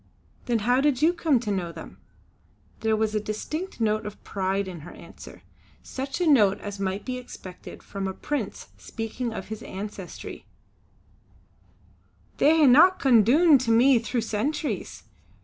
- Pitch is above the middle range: Yes, high, 225 Hz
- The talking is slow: No, average, 155 wpm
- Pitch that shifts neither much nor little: Yes, average, 5.0 semitones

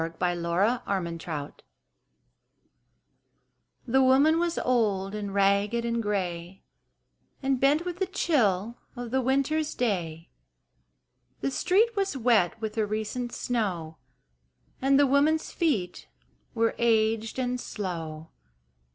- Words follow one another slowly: Yes, slow, 115 wpm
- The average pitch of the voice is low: No, high, 225 Hz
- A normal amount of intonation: No, wide, 6.1 semitones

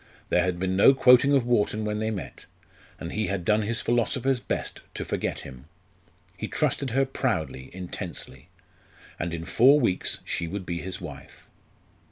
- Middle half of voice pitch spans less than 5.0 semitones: No, wide, 5.6 semitones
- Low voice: Yes, low, 105 Hz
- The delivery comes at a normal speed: Yes, average, 170 wpm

